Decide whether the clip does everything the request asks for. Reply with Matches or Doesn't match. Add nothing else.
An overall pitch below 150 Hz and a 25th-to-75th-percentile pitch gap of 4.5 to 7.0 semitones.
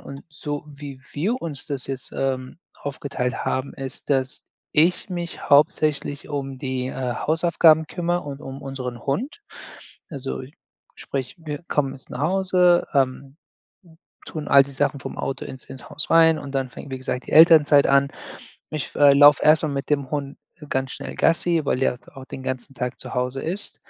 Doesn't match